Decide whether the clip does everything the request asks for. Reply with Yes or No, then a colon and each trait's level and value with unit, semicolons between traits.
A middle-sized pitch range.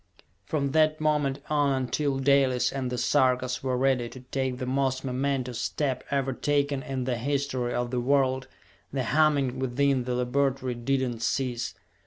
No: narrow, 1.9 semitones